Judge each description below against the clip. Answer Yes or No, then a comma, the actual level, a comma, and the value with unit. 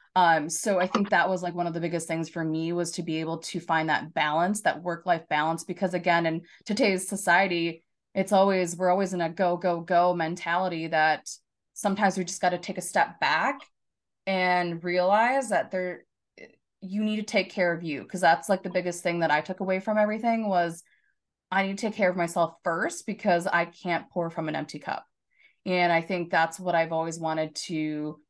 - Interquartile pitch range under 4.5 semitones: Yes, narrow, 2.4 semitones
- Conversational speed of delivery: No, fast, 210 wpm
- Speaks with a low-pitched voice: No, medium, 175 Hz